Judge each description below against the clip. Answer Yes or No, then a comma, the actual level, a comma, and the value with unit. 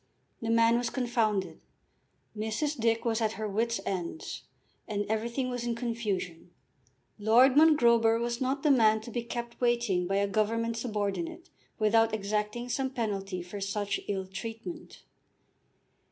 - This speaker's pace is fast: No, average, 140 wpm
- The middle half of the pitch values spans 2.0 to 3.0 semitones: Yes, narrow, 2.6 semitones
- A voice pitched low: No, high, 225 Hz